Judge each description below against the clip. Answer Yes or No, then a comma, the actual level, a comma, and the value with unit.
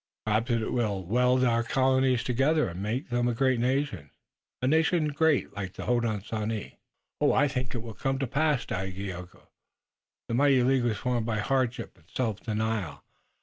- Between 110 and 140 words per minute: No, average, 170 wpm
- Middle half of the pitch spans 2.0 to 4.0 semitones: Yes, average, 3.7 semitones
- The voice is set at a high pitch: No, low, 120 Hz